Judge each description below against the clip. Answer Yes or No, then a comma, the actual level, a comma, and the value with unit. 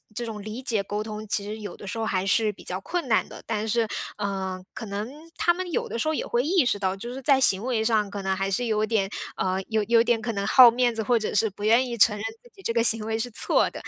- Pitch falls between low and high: No, high, 220 Hz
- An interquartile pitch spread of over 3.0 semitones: No, average, 2.7 semitones